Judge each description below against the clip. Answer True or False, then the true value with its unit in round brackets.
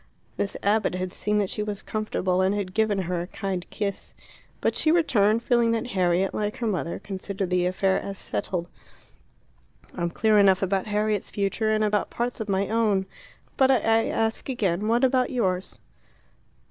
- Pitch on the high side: True (205 Hz)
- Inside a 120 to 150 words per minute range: False (170 wpm)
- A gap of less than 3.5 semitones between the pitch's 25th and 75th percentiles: True (2.9 semitones)